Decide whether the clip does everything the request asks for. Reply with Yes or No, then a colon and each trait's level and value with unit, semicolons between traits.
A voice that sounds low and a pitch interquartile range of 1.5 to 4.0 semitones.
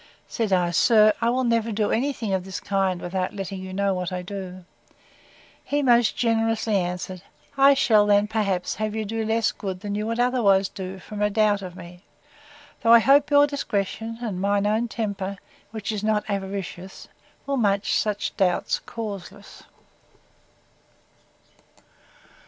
No: high, 205 Hz; average, 2.9 semitones